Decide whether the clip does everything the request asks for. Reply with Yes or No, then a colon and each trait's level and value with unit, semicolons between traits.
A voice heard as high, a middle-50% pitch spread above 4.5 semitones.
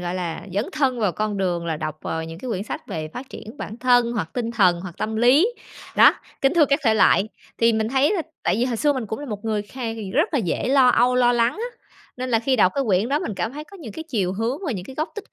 Yes: high, 230 Hz; average, 5.0 semitones